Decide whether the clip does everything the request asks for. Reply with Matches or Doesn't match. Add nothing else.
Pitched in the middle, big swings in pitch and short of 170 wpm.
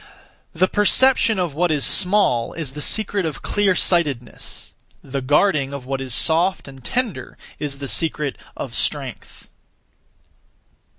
Matches